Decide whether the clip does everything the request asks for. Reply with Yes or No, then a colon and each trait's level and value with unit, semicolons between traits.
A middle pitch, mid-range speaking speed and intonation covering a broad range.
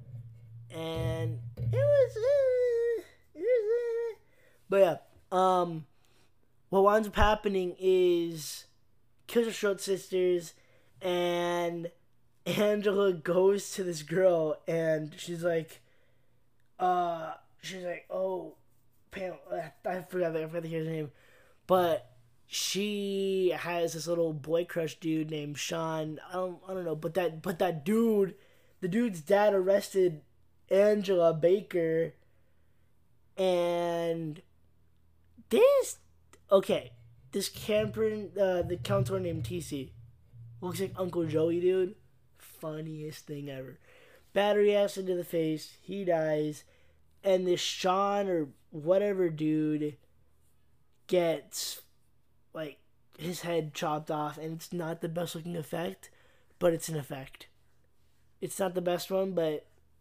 No: medium, 170 Hz; slow, 120 wpm; wide, 6.2 semitones